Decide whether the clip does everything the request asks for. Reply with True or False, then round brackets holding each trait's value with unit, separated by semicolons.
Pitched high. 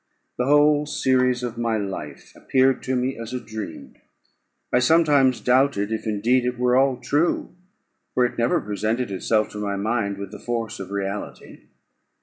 False (120 Hz)